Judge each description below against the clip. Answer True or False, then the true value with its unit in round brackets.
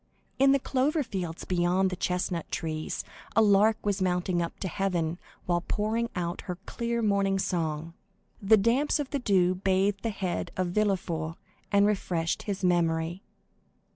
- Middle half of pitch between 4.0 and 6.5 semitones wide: False (3.3 semitones)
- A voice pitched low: False (190 Hz)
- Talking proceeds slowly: False (155 wpm)